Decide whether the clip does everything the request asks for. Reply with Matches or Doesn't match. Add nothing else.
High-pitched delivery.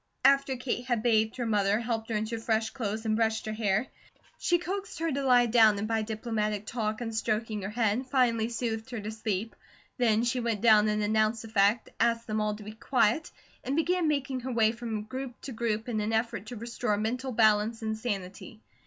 Matches